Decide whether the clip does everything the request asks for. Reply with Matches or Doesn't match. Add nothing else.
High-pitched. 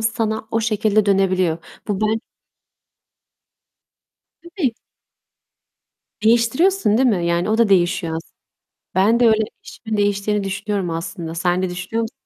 Matches